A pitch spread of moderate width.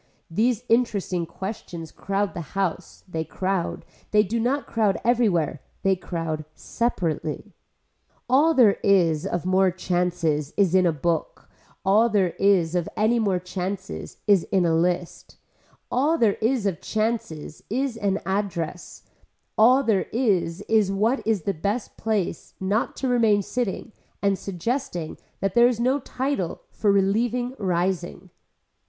Yes: average, 4.4 semitones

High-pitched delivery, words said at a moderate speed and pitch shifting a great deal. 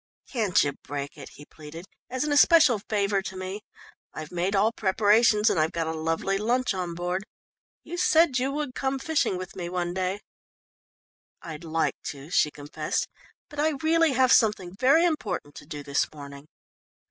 Yes: high, 195 Hz; average, 175 wpm; wide, 7.8 semitones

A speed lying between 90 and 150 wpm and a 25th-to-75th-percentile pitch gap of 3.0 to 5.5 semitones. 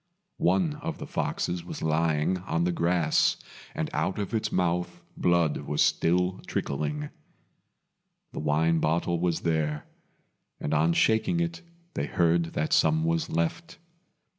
No: average, 140 wpm; narrow, 2.5 semitones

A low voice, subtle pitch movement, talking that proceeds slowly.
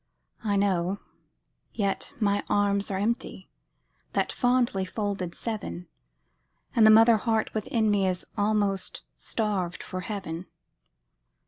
No: high, 205 Hz; narrow, 2.3 semitones; slow, 115 wpm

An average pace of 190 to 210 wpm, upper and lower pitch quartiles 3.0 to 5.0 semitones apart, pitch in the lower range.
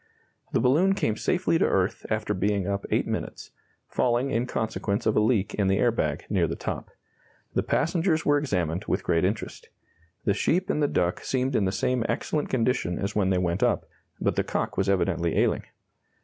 No: average, 195 wpm; wide, 5.4 semitones; low, 105 Hz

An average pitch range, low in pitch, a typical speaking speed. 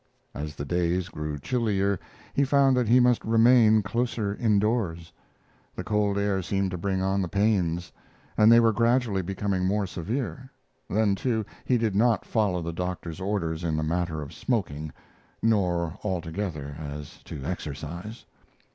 Yes: average, 4.7 semitones; low, 100 Hz; average, 155 wpm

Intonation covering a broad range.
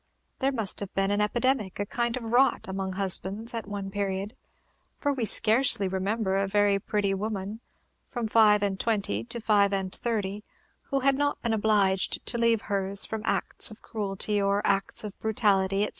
No: narrow, 2.5 semitones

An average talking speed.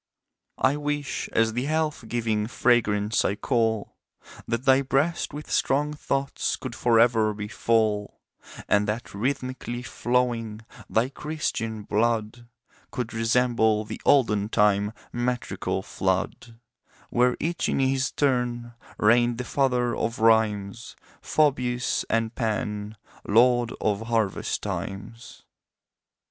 No: slow, 115 wpm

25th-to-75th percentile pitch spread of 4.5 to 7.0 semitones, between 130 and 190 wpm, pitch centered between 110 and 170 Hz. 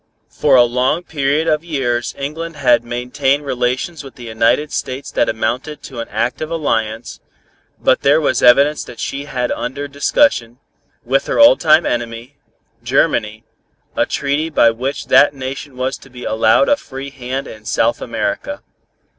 No: average, 3.4 semitones; average, 160 wpm; low, 135 Hz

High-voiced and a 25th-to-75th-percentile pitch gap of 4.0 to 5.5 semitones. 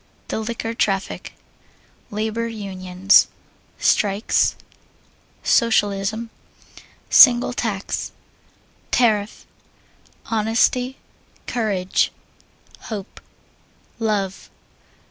No: high, 215 Hz; average, 2.7 semitones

